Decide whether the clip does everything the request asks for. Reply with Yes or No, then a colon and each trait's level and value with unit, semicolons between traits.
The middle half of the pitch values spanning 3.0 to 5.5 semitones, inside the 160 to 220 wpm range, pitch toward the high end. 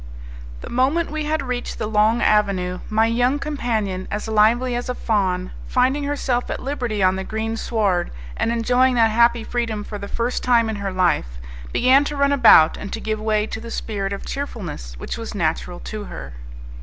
Yes: average, 3.7 semitones; average, 195 wpm; high, 225 Hz